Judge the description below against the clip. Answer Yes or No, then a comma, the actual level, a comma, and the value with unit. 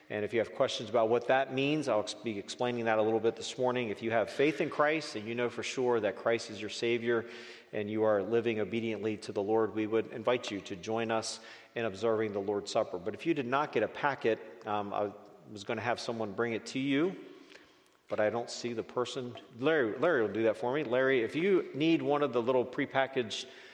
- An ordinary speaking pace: No, fast, 240 wpm